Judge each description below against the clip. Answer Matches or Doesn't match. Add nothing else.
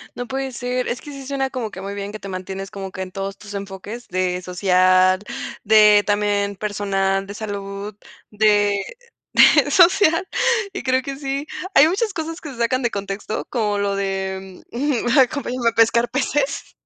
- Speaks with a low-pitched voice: Doesn't match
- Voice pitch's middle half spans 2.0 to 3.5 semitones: Doesn't match